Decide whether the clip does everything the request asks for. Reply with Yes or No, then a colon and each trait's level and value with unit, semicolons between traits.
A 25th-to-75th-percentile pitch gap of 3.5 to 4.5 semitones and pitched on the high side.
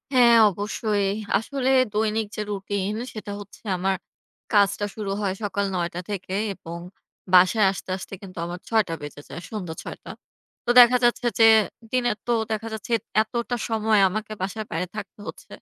No: average, 2.7 semitones; high, 205 Hz